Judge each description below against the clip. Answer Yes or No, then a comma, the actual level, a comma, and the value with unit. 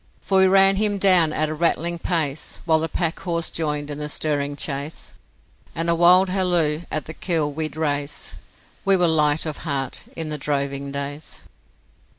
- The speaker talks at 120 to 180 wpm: Yes, average, 170 wpm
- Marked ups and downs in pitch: No, average, 2.8 semitones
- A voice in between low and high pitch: Yes, medium, 155 Hz